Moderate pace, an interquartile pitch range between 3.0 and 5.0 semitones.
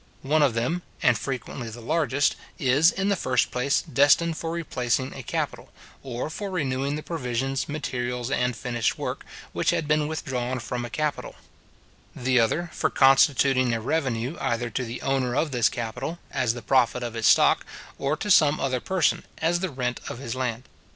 Yes: average, 180 wpm; average, 3.7 semitones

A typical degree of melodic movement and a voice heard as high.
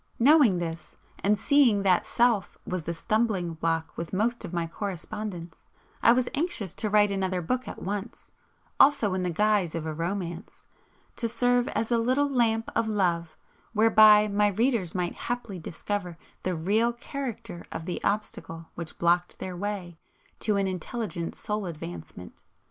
Yes: average, 4.8 semitones; high, 200 Hz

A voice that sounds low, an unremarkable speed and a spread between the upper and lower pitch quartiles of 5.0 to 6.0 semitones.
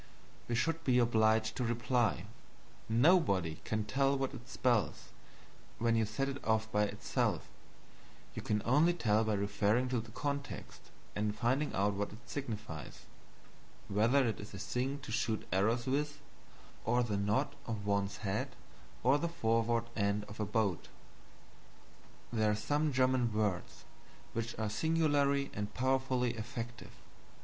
No: low, 115 Hz; average, 145 wpm; average, 3.8 semitones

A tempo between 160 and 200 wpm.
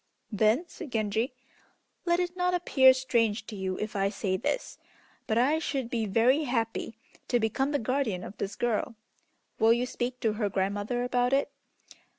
Yes: average, 170 wpm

